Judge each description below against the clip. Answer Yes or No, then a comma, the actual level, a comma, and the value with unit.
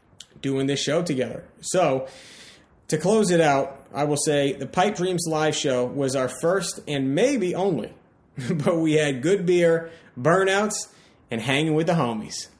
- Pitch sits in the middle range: Yes, medium, 155 Hz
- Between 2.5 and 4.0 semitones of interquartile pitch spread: No, average, 4.6 semitones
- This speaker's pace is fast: No, average, 160 wpm